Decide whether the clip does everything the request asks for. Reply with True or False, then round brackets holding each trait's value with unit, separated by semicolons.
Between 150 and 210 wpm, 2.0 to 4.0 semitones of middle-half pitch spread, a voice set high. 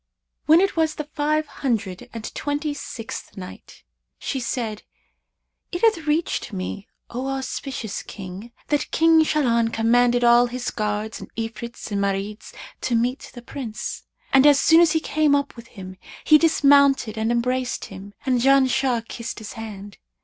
False (155 wpm; 4.7 semitones; 245 Hz)